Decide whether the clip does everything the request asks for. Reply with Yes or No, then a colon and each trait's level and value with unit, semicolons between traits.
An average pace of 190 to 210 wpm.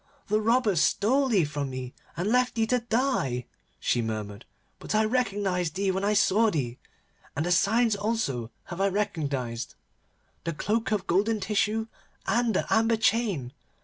No: average, 160 wpm